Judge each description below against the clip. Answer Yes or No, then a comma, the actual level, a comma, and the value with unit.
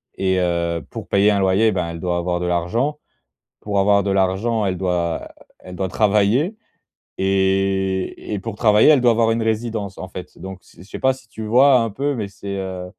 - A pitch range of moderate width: Yes, average, 3.2 semitones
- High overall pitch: No, low, 100 Hz